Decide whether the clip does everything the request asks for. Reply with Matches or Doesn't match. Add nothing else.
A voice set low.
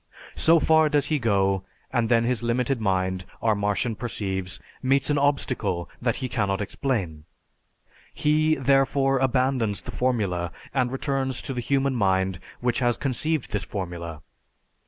Matches